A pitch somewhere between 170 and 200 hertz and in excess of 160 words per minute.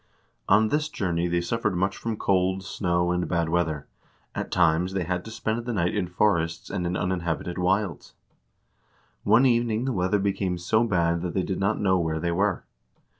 No: very low, 90 Hz; average, 185 wpm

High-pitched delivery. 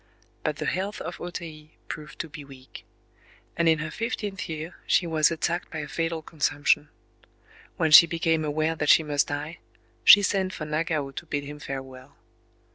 No: medium, 155 Hz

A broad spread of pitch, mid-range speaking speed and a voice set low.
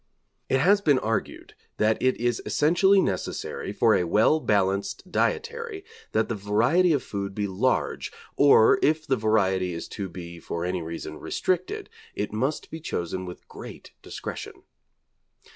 Yes: wide, 8.5 semitones; average, 150 wpm; low, 110 Hz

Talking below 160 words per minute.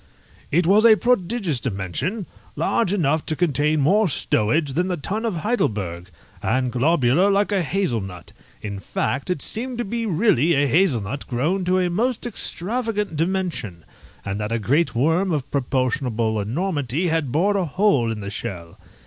No: average, 165 wpm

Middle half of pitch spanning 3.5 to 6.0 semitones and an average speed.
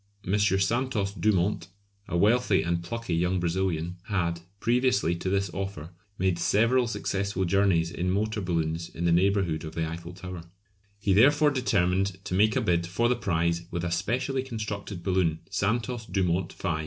Yes: average, 3.8 semitones; average, 165 wpm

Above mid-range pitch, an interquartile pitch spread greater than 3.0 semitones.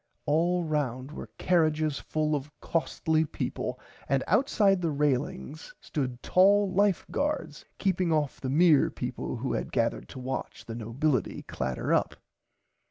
No: medium, 155 Hz; average, 4.7 semitones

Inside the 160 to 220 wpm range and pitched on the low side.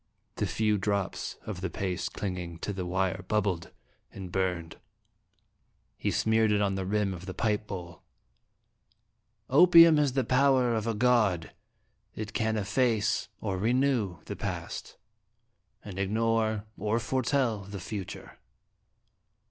No: slow, 135 wpm; low, 105 Hz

